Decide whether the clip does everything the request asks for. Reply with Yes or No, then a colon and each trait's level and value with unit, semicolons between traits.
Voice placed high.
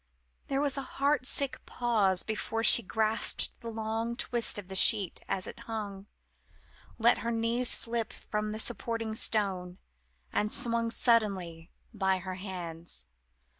Yes: high, 220 Hz